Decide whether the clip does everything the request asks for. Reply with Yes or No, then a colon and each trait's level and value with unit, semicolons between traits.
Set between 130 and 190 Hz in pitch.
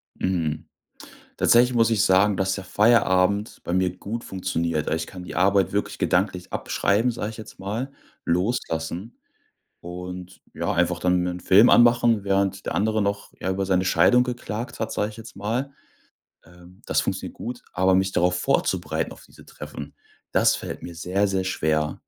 No: very low, 95 Hz